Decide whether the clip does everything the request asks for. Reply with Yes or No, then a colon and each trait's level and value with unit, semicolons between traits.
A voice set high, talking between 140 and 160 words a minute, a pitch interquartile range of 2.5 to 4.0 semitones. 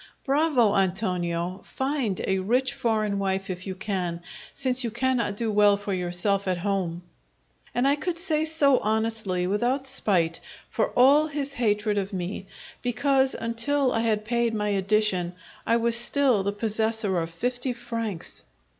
No: high, 220 Hz; average, 155 wpm; average, 4.6 semitones